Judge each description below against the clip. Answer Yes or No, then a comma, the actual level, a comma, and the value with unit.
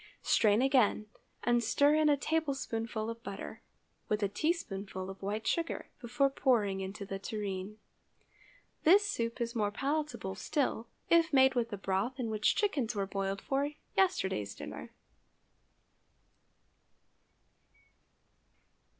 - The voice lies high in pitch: Yes, high, 230 Hz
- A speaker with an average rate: No, slow, 125 wpm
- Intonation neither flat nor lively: No, wide, 5.8 semitones